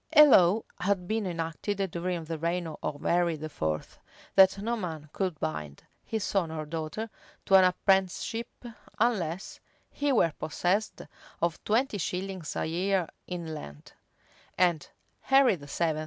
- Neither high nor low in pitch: Yes, medium, 180 Hz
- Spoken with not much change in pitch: No, average, 3.8 semitones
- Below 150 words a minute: Yes, average, 140 wpm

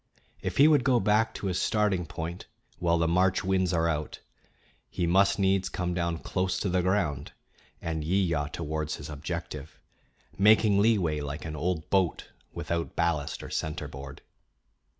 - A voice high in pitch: No, very low, 85 Hz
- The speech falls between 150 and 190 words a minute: Yes, average, 155 wpm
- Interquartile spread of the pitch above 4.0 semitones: No, average, 3.5 semitones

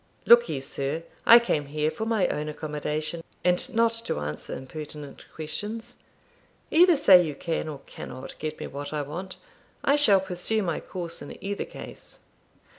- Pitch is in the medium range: Yes, medium, 165 Hz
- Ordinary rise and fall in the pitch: No, wide, 6.3 semitones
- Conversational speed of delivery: Yes, average, 170 wpm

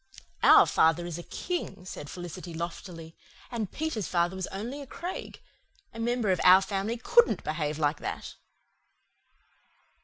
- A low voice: No, medium, 185 Hz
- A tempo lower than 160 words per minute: Yes, average, 145 wpm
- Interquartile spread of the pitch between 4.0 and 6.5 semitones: Yes, wide, 5.5 semitones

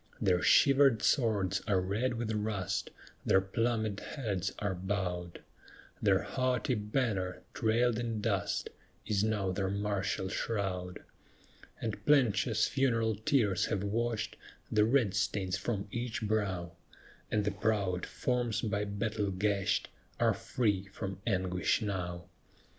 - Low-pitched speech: Yes, low, 105 Hz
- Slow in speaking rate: Yes, slow, 125 wpm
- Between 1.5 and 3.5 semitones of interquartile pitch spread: Yes, average, 3.0 semitones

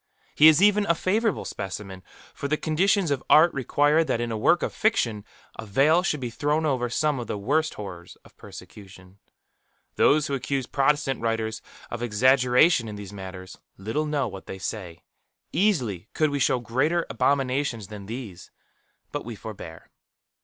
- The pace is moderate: Yes, average, 165 wpm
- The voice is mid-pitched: No, low, 130 Hz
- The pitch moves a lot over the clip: Yes, wide, 6.5 semitones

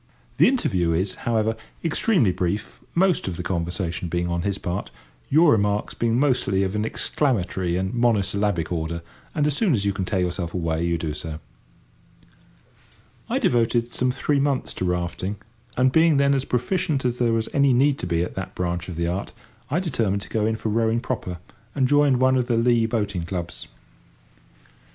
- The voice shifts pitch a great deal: Yes, wide, 6.3 semitones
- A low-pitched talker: Yes, low, 105 Hz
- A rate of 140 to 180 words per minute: No, average, 190 wpm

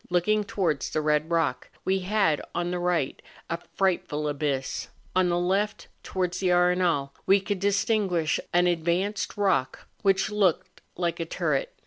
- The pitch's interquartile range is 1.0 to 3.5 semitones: Yes, average, 3.0 semitones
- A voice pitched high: No, medium, 180 Hz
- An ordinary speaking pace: Yes, average, 155 wpm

